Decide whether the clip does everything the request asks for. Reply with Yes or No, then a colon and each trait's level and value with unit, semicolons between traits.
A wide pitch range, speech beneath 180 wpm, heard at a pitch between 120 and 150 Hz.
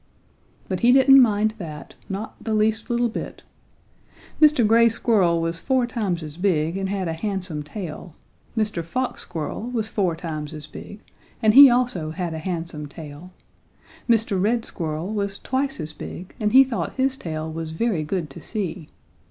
No: wide, 5.8 semitones; average, 170 wpm; high, 195 Hz